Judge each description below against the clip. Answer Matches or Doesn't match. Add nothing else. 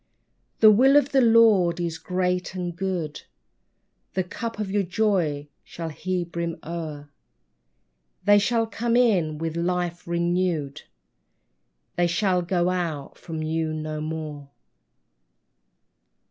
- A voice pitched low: Doesn't match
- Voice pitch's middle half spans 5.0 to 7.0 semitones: Doesn't match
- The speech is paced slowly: Matches